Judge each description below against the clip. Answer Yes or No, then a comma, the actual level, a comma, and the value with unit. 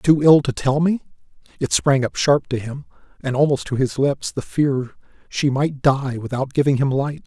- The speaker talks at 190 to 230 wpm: Yes, fast, 205 wpm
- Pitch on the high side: No, medium, 140 Hz